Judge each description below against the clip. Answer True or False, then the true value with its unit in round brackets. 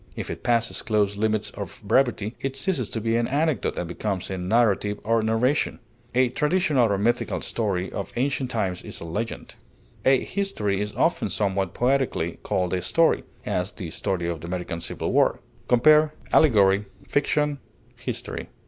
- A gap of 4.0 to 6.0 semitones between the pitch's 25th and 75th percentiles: True (5.3 semitones)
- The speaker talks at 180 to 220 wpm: False (165 wpm)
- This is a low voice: True (110 Hz)